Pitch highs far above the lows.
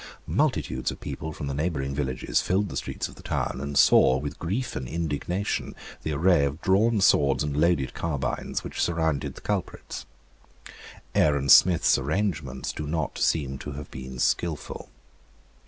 No: average, 3.7 semitones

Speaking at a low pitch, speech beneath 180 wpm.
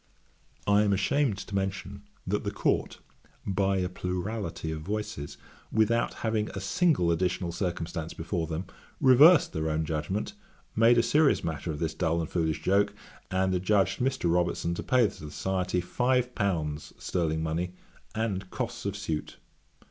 Yes: very low, 95 Hz; average, 155 wpm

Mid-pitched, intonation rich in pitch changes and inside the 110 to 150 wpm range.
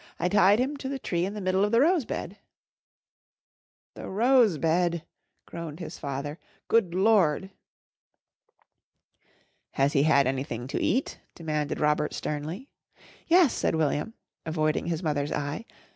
Yes: medium, 170 Hz; wide, 6.0 semitones; average, 140 wpm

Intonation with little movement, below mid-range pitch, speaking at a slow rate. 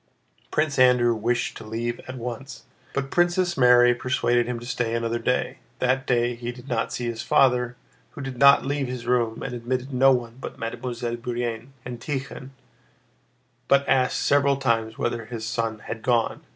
No: narrow, 2.0 semitones; low, 125 Hz; average, 175 wpm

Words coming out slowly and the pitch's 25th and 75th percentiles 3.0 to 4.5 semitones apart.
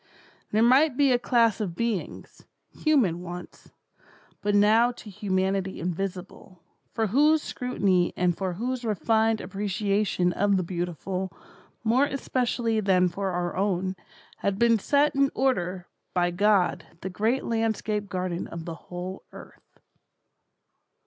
Yes: slow, 130 wpm; average, 4.2 semitones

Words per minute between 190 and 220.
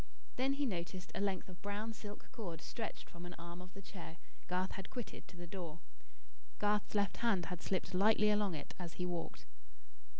Yes: average, 195 wpm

